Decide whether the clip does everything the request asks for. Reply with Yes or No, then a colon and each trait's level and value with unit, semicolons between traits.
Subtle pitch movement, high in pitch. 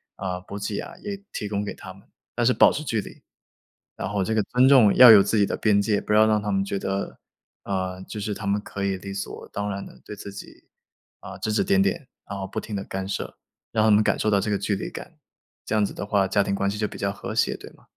No: narrow, 1.6 semitones; low, 100 Hz